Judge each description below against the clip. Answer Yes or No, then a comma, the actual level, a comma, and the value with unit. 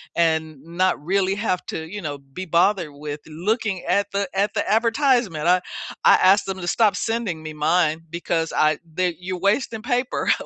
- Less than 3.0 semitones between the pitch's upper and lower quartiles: No, average, 4.2 semitones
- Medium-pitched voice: Yes, medium, 180 Hz